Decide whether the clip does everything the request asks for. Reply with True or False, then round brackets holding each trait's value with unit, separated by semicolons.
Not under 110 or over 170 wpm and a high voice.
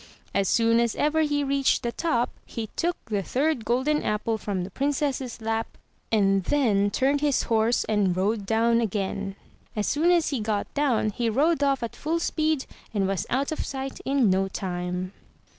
False (180 wpm; 235 Hz)